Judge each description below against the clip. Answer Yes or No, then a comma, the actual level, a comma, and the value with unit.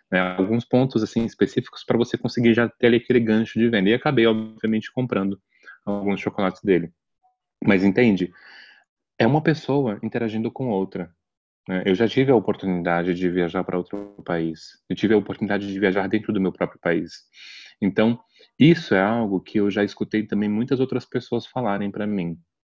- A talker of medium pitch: No, low, 105 Hz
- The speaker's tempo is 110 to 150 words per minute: No, average, 175 wpm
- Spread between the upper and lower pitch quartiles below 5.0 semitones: Yes, average, 3.6 semitones